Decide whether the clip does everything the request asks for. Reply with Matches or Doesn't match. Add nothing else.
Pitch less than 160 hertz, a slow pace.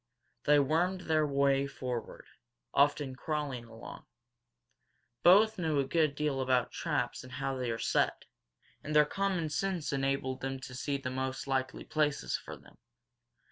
Doesn't match